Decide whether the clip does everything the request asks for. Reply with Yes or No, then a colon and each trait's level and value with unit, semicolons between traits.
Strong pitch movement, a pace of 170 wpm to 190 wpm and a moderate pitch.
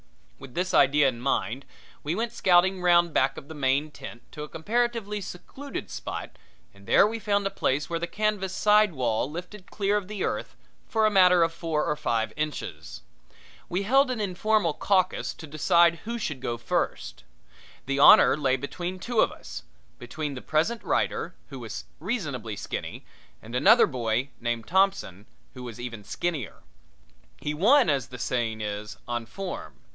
Yes: wide, 7.5 semitones; average, 175 wpm; medium, 160 Hz